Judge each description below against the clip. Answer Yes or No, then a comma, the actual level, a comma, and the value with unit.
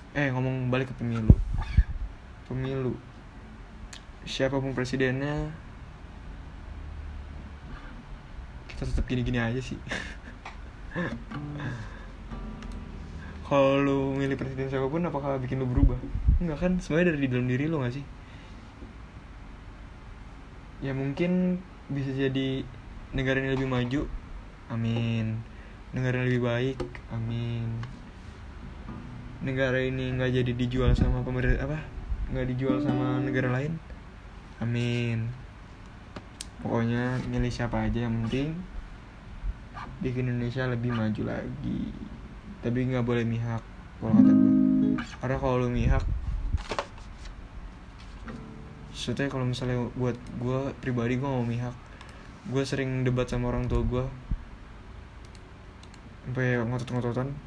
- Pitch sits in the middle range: No, low, 125 Hz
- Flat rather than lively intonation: No, average, 3.3 semitones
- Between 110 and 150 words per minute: No, average, 100 wpm